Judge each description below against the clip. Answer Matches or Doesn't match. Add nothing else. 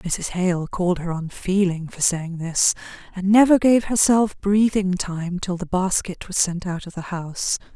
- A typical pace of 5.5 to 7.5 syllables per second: Doesn't match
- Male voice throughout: Doesn't match